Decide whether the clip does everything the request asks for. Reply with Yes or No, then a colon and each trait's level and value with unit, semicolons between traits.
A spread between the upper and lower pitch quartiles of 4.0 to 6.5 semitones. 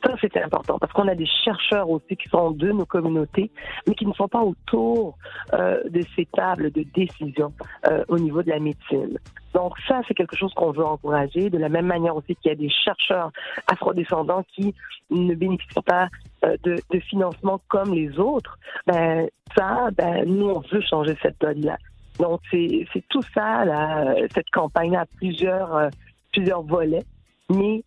No: average, 3.5 semitones